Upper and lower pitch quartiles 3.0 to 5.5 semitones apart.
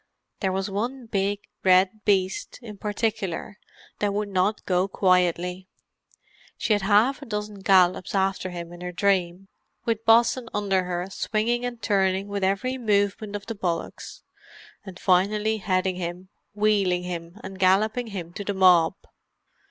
No: narrow, 2.4 semitones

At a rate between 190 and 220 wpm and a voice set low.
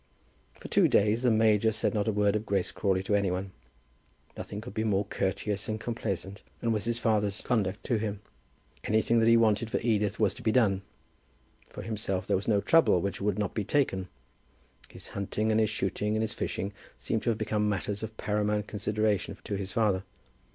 Yes: average, 200 wpm; low, 105 Hz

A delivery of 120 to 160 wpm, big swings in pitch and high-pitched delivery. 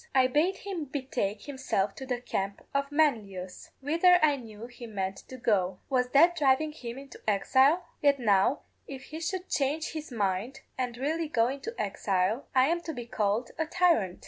No: average, 180 wpm; wide, 5.8 semitones; very high, 260 Hz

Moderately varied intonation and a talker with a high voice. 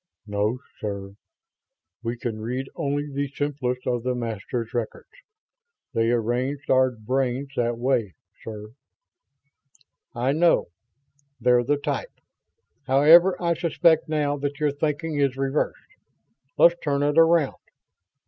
No: average, 3.5 semitones; low, 135 Hz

